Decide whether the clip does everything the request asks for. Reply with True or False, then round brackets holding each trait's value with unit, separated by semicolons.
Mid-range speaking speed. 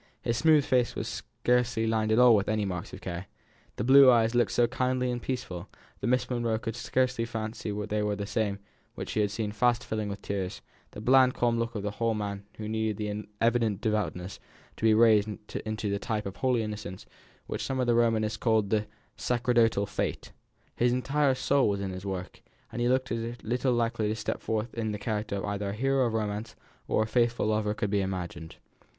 False (220 wpm)